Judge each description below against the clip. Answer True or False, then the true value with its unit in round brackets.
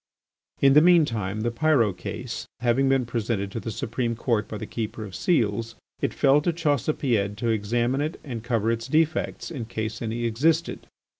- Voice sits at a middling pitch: False (120 Hz)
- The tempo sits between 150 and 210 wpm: True (180 wpm)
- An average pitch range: True (3.9 semitones)